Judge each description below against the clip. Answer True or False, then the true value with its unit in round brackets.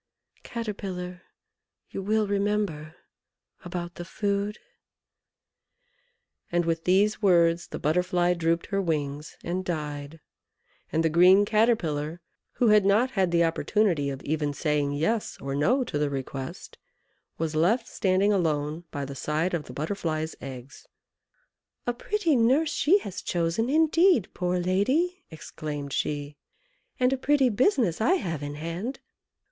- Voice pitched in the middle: True (180 Hz)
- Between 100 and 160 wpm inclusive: True (140 wpm)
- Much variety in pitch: True (5.7 semitones)